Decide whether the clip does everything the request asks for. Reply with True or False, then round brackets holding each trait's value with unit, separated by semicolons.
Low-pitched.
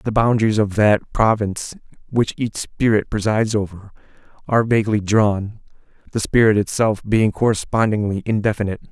True (105 Hz)